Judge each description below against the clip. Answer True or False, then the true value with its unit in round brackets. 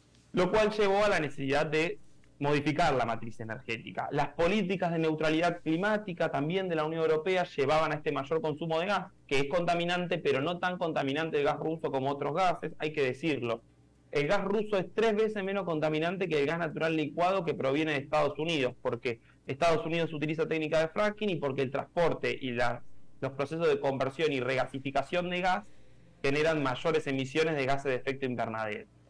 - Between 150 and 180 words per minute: False (190 wpm)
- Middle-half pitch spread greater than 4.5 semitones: False (4.2 semitones)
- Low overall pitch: False (155 Hz)